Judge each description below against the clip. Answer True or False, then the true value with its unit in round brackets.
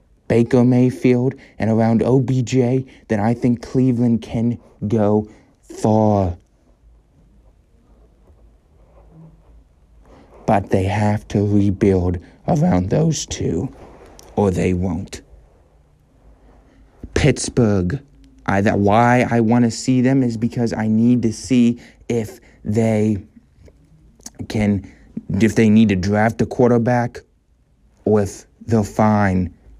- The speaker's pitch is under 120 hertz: True (110 Hz)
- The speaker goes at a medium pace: False (105 wpm)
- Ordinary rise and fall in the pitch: True (3.4 semitones)